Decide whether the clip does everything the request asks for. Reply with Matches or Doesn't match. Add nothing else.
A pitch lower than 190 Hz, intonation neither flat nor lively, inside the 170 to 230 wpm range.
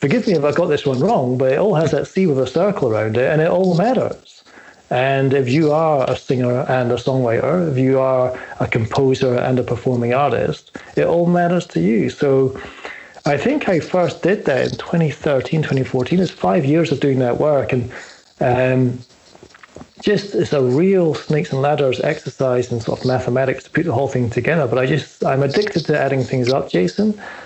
Matches